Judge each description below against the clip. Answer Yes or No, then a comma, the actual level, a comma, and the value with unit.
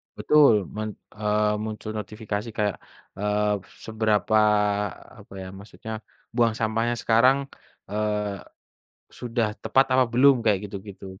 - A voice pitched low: Yes, low, 110 Hz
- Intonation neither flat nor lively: No, narrow, 1.9 semitones